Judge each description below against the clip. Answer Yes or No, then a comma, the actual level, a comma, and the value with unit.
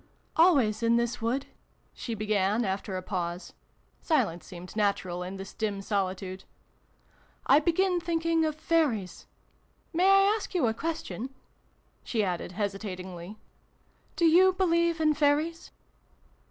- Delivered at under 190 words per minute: Yes, average, 140 wpm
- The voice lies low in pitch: No, high, 230 Hz